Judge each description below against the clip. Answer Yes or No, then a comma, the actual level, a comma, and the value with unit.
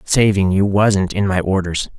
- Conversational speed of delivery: Yes, average, 180 wpm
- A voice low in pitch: Yes, very low, 95 Hz